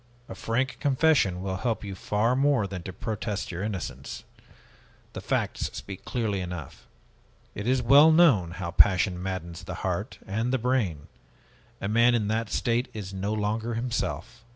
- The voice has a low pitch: Yes, low, 105 Hz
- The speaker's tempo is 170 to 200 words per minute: No, average, 160 wpm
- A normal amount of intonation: Yes, average, 4.3 semitones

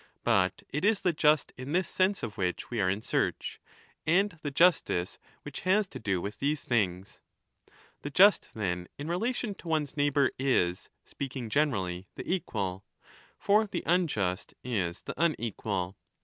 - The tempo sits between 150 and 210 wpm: Yes, average, 160 wpm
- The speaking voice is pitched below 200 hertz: Yes, low, 135 Hz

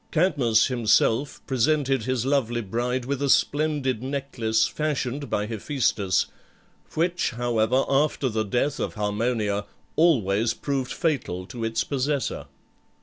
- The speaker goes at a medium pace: No, slow, 120 wpm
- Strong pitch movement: No, average, 4.0 semitones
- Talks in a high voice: No, low, 125 Hz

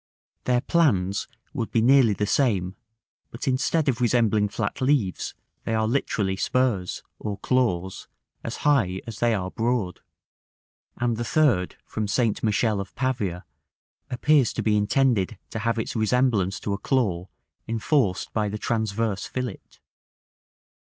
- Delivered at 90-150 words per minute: Yes, average, 140 wpm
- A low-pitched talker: Yes, low, 110 Hz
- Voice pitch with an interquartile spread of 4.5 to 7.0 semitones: No, average, 4.0 semitones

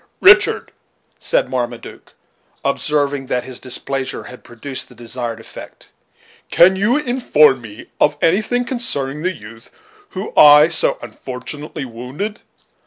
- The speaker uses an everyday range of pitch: No, wide, 7.1 semitones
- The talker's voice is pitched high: No, medium, 140 Hz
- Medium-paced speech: No, slow, 120 wpm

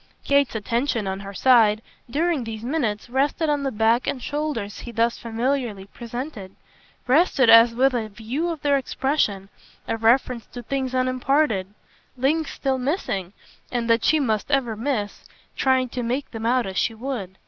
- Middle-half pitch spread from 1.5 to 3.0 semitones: No, average, 3.7 semitones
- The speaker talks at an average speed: Yes, average, 165 wpm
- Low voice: No, high, 245 Hz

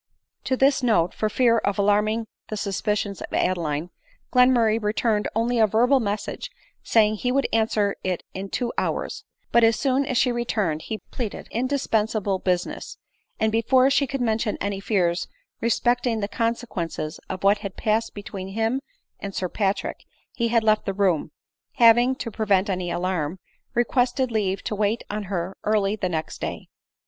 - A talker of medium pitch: No, high, 215 Hz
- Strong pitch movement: No, average, 3.2 semitones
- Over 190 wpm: No, average, 170 wpm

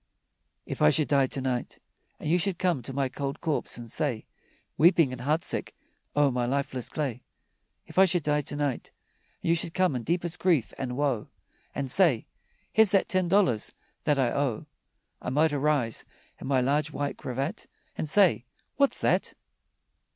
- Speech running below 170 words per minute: No, average, 175 wpm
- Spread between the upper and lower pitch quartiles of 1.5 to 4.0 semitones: No, average, 4.5 semitones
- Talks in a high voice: No, medium, 145 Hz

